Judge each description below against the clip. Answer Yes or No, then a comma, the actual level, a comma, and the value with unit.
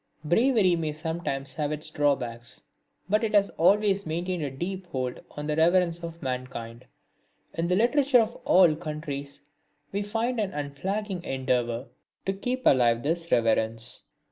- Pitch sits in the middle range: Yes, medium, 165 Hz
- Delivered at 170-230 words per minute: No, average, 145 wpm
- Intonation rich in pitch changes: Yes, wide, 6.1 semitones